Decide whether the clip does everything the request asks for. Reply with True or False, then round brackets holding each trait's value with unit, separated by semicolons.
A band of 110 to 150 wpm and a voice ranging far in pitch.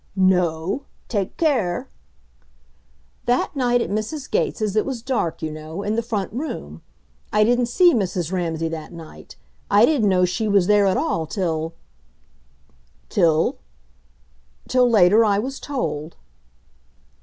True (140 wpm; 6.2 semitones)